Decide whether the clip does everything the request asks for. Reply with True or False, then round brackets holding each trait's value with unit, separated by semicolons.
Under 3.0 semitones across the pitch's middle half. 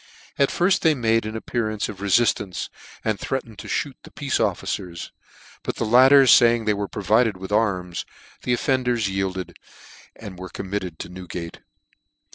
False (4.3 semitones)